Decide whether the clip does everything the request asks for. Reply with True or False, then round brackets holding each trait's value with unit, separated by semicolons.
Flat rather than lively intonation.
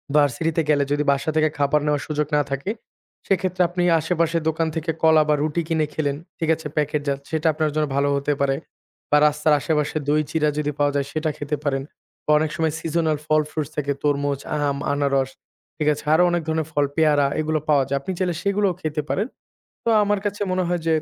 True (1.9 semitones)